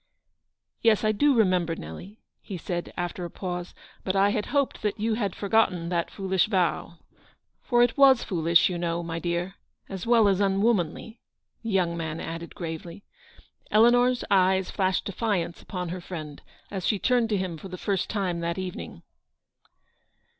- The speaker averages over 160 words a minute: Yes, average, 170 wpm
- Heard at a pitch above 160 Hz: Yes, high, 190 Hz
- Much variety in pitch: No, average, 3.7 semitones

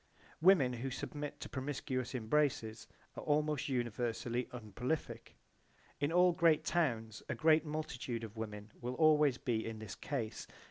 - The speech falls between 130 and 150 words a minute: Yes, average, 140 wpm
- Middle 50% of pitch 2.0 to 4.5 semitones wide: No, average, 4.9 semitones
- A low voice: Yes, low, 130 Hz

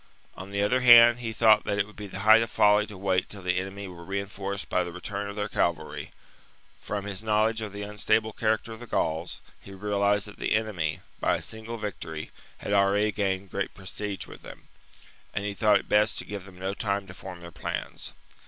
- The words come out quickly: Yes, fast, 220 wpm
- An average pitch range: No, narrow, 1.8 semitones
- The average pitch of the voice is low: Yes, low, 100 Hz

